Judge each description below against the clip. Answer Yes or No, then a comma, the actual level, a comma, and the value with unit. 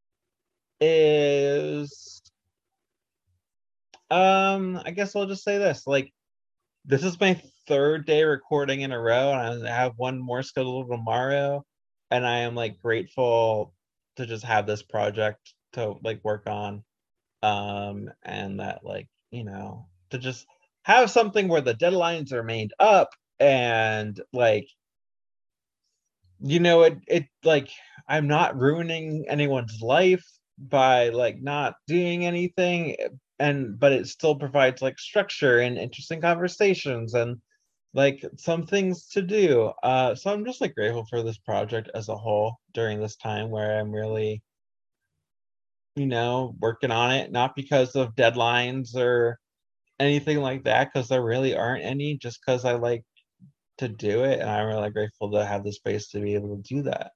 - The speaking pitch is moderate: No, low, 130 Hz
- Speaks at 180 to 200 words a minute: No, average, 150 wpm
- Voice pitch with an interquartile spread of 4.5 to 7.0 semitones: Yes, wide, 5.4 semitones